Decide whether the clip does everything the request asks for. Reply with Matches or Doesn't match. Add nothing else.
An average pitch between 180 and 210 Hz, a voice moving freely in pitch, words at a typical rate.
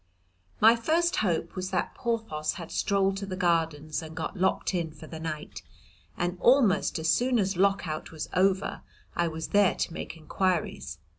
Doesn't match